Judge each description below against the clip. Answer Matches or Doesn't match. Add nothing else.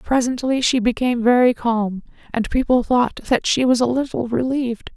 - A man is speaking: Doesn't match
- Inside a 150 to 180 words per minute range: Matches